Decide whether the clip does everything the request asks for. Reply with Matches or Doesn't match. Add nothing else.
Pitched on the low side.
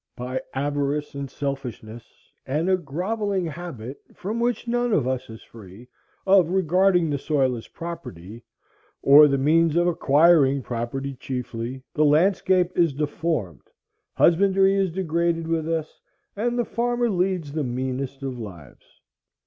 Doesn't match